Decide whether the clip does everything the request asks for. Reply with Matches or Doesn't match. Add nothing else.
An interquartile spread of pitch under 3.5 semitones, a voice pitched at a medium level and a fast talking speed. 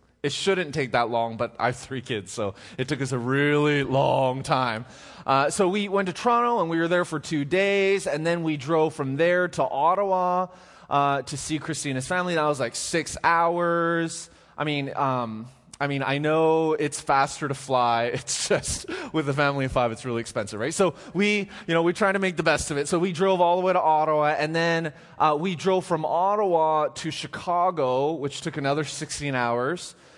Doesn't match